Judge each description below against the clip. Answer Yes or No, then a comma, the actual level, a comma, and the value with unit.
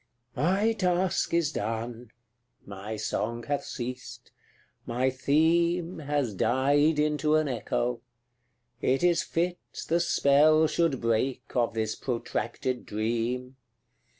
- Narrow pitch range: No, average, 5.3 semitones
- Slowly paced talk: Yes, slow, 115 wpm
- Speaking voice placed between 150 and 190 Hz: No, low, 135 Hz